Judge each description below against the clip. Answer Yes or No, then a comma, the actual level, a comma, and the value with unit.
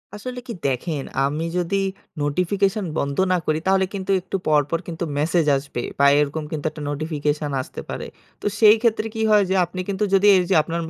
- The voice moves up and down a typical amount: Yes, average, 4.7 semitones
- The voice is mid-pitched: Yes, medium, 170 Hz